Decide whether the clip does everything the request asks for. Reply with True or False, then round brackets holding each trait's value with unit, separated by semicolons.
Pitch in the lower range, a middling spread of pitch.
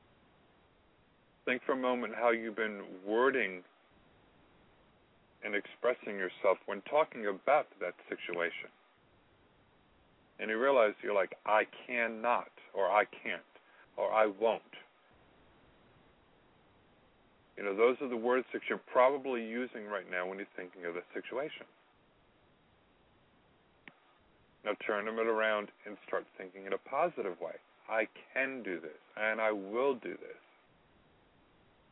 True (110 Hz; 3.3 semitones)